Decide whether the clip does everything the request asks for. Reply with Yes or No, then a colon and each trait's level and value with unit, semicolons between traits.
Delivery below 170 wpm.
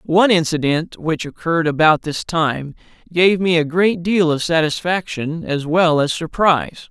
Yes: average, 155 wpm